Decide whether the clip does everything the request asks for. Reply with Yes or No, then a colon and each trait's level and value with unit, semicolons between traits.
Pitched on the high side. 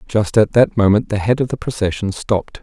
No: low, 110 Hz